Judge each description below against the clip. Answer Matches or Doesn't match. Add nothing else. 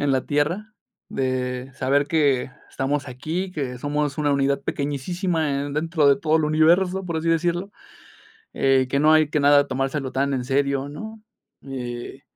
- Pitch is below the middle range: Doesn't match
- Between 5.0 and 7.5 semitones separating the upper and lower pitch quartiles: Doesn't match